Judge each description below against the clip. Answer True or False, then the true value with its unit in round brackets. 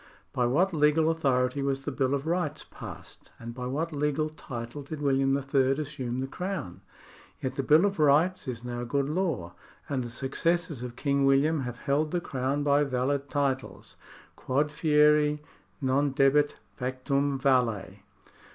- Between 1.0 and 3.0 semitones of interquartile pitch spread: True (2.6 semitones)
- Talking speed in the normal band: True (160 wpm)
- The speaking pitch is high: False (140 Hz)